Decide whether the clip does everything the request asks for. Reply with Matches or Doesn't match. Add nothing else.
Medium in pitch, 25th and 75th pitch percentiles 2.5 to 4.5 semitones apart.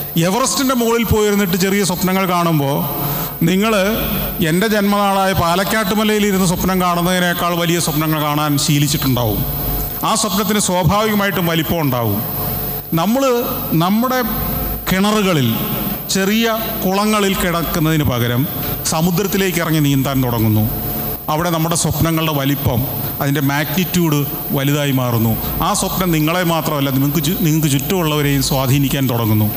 Doesn't match